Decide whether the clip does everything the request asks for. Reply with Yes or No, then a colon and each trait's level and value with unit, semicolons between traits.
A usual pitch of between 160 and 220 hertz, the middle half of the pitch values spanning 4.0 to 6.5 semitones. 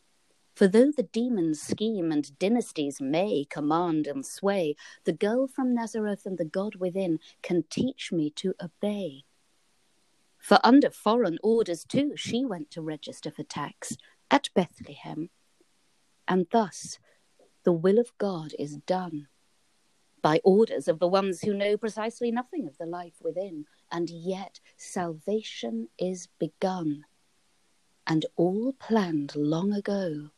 Yes: medium, 185 Hz; wide, 5.4 semitones